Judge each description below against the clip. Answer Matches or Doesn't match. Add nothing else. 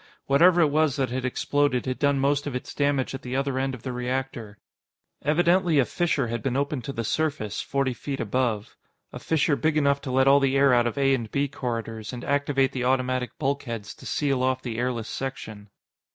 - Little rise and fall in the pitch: Matches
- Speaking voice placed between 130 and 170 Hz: Matches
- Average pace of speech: Doesn't match